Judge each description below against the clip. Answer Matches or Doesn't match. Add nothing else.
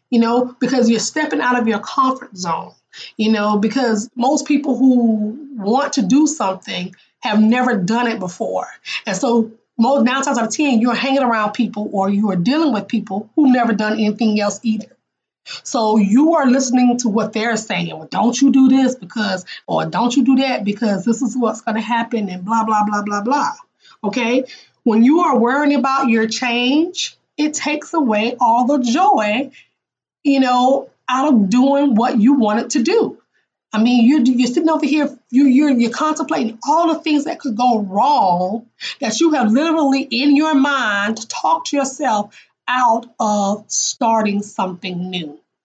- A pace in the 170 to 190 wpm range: Matches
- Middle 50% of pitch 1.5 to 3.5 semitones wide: Doesn't match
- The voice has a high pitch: Matches